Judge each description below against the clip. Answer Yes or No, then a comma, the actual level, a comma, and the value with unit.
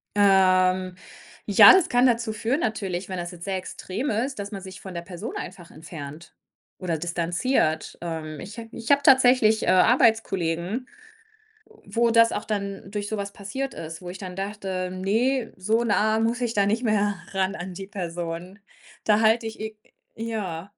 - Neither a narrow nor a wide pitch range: Yes, average, 3.7 semitones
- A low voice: No, high, 200 Hz